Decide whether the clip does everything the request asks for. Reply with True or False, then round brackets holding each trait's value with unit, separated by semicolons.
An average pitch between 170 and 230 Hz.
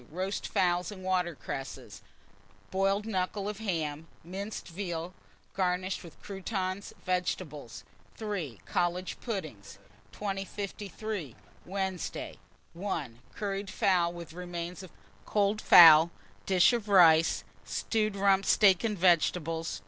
True (185 Hz)